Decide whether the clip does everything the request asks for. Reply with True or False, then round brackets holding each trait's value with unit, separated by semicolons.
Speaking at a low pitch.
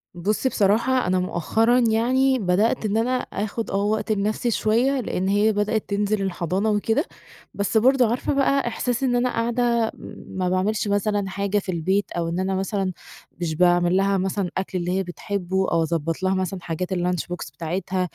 False (200 Hz)